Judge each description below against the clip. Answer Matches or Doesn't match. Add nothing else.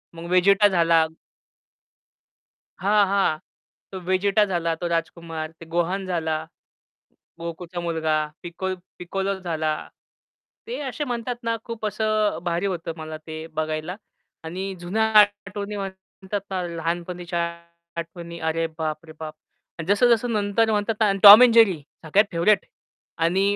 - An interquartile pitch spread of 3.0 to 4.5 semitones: Matches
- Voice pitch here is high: Doesn't match